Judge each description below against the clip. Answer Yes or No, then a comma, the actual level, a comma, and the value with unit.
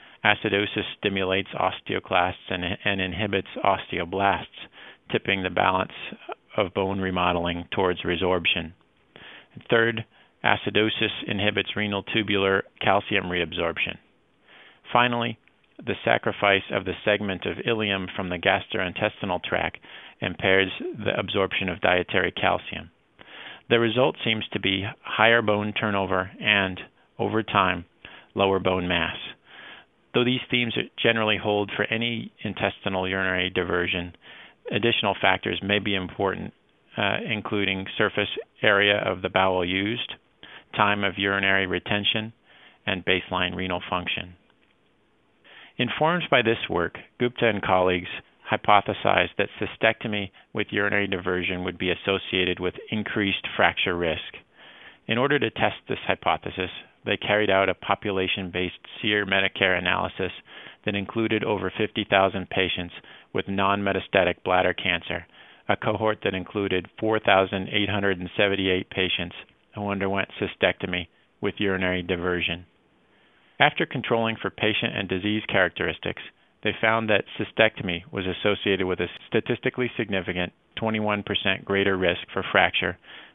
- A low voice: Yes, low, 100 Hz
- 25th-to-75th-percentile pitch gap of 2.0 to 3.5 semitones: Yes, narrow, 2.4 semitones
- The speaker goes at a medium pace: No, slow, 120 wpm